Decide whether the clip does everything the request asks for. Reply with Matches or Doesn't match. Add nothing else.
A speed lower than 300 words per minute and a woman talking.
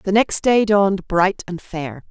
Matches